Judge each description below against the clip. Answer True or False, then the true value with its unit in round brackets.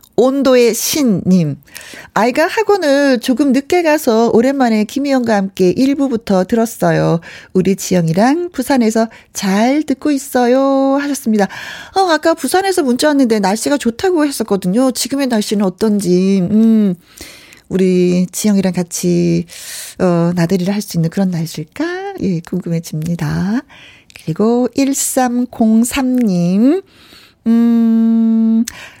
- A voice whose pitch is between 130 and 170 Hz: False (225 Hz)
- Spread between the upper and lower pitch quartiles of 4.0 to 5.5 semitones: False (6.3 semitones)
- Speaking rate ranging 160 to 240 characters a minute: False (255 characters per minute)